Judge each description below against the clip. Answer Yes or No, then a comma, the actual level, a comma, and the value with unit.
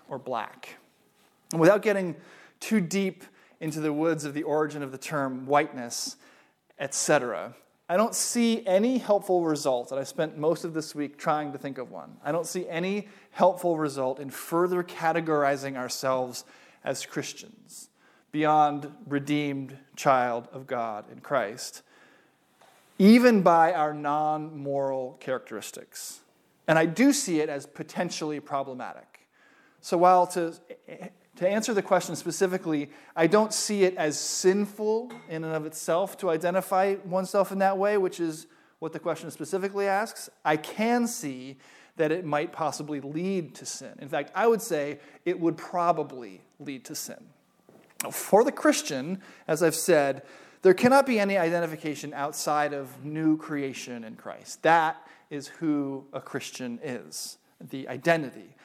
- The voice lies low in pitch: No, medium, 160 Hz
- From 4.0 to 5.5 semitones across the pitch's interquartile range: Yes, average, 4.7 semitones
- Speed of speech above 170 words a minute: No, average, 150 wpm